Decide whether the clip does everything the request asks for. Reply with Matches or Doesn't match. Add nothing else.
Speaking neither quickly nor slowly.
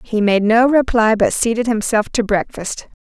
Matches